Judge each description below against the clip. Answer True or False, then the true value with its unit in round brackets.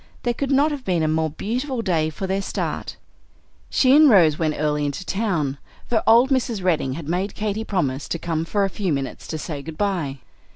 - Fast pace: True (210 wpm)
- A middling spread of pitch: False (6.2 semitones)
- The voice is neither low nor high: True (180 Hz)